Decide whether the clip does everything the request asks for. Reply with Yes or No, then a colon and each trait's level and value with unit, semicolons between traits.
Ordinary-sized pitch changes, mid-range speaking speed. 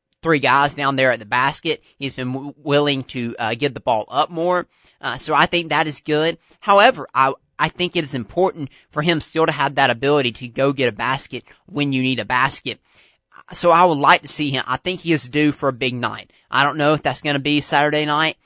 No: average, 3.0 semitones; fast, 240 wpm